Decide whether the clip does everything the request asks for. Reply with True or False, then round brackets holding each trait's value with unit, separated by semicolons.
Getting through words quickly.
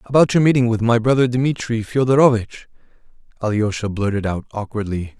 False (140 wpm)